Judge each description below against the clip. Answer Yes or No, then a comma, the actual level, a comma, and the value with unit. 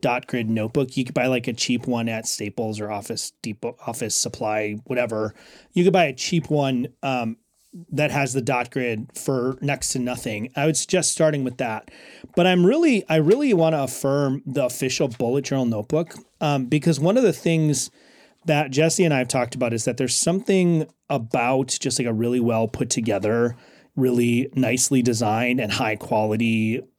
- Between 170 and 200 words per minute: Yes, average, 185 wpm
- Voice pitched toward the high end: No, low, 130 Hz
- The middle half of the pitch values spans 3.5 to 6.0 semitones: Yes, average, 4.3 semitones